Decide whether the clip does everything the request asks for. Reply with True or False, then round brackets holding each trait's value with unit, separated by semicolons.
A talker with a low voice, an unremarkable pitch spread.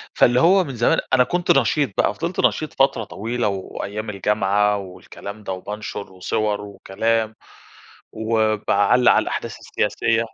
True (110 Hz; 3.3 semitones)